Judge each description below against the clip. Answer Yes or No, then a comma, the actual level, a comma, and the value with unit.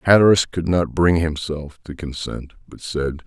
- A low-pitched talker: Yes, very low, 80 Hz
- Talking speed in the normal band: Yes, average, 165 wpm